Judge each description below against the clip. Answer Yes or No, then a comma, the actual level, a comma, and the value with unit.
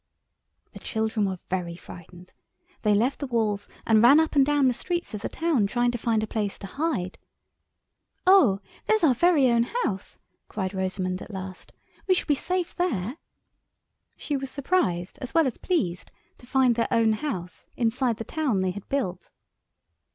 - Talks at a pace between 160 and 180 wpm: Yes, average, 175 wpm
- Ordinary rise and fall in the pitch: No, wide, 6.7 semitones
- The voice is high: Yes, high, 230 Hz